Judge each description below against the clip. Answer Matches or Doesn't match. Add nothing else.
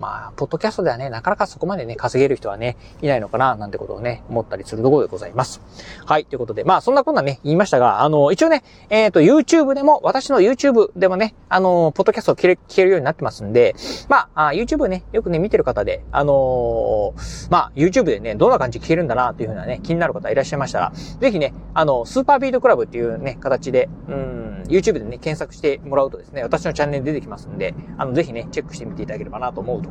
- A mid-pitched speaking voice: Matches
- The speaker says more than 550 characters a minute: Matches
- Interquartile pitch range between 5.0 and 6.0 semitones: Doesn't match